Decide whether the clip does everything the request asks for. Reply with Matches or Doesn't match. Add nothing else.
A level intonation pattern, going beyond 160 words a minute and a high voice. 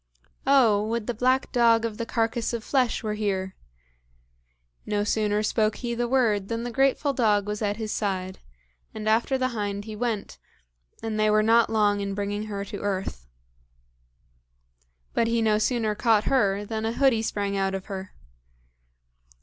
Matches